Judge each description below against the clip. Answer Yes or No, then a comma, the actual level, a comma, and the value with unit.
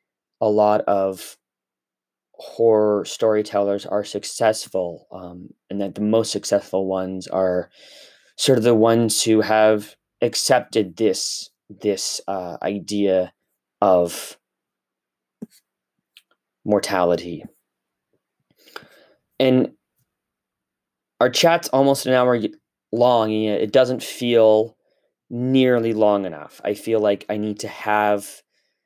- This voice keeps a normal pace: No, slow, 100 wpm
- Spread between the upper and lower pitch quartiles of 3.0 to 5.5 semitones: No, narrow, 2.4 semitones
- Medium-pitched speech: No, low, 105 Hz